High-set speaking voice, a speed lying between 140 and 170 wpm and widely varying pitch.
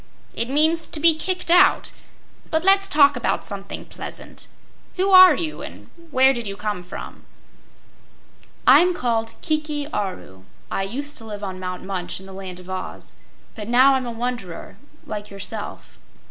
Yes: high, 235 Hz; average, 160 wpm; wide, 7.8 semitones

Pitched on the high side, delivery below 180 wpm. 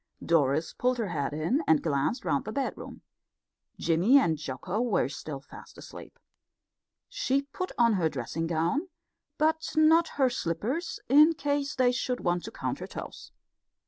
Yes: high, 230 Hz; average, 155 wpm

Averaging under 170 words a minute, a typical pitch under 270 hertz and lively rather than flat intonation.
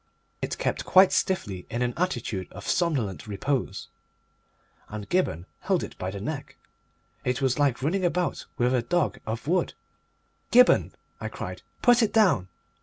Yes: average, 155 wpm; low, 135 Hz; wide, 8.5 semitones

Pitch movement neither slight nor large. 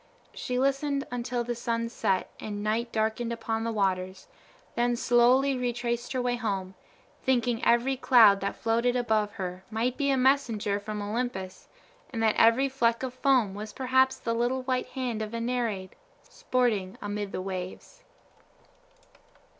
Yes: average, 3.1 semitones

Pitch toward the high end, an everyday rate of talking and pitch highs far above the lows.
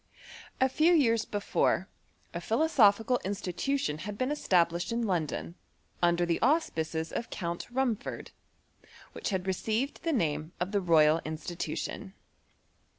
No: high, 195 Hz; slow, 125 wpm; wide, 6.2 semitones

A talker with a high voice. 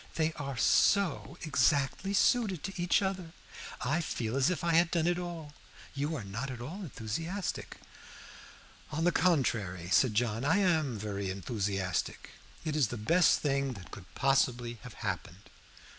No: medium, 140 Hz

